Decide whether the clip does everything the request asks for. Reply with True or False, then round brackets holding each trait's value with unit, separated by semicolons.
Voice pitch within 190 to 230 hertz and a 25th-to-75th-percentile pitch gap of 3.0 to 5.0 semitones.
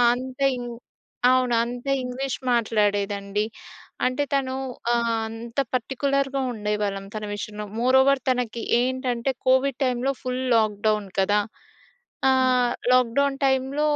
False (245 Hz; 3.5 semitones)